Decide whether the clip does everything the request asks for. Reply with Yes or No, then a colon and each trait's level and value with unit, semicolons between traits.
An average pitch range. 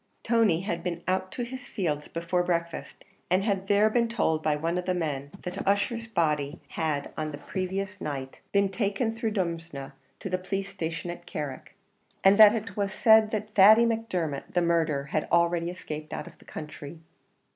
Yes: average, 4.2 semitones